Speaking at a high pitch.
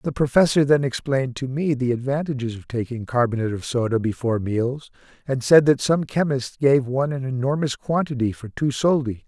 No: low, 130 Hz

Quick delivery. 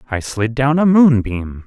No: average, 180 wpm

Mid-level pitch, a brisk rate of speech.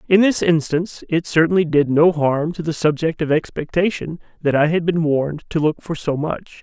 Yes: medium, 160 Hz; fast, 210 wpm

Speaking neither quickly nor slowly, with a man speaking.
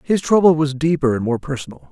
No: fast, 220 wpm; male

